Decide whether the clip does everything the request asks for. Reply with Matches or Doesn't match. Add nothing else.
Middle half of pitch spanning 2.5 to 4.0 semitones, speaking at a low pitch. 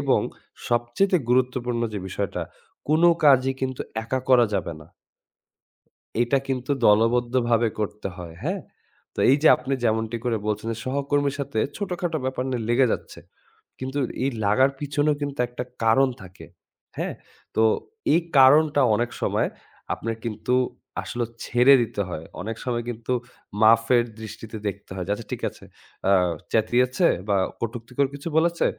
Matches